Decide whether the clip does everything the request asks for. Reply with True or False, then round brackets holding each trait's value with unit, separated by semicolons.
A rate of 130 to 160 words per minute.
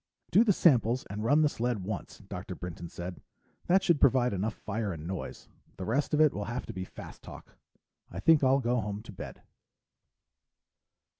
False (190 wpm)